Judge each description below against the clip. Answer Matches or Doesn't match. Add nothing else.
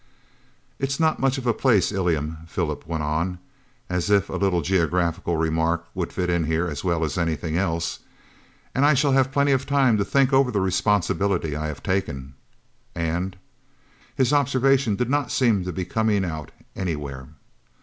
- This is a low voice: Matches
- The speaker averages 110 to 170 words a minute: Doesn't match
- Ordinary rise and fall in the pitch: Doesn't match